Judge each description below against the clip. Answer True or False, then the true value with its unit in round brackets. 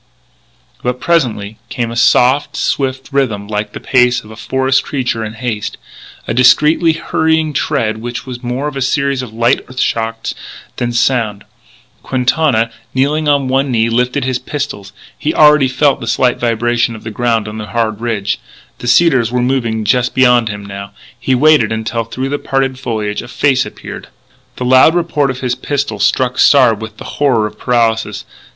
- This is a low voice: True (125 Hz)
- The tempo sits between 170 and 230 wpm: True (175 wpm)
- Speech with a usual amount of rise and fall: True (3.1 semitones)